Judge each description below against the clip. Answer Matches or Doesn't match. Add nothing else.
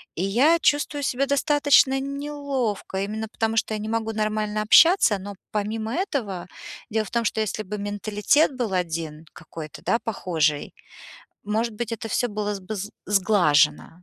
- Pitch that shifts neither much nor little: Matches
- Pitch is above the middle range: Matches